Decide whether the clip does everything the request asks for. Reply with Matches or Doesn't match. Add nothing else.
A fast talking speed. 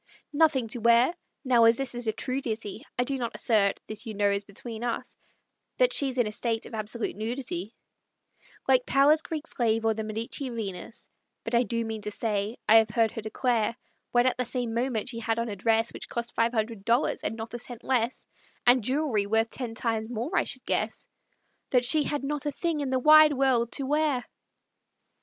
Matches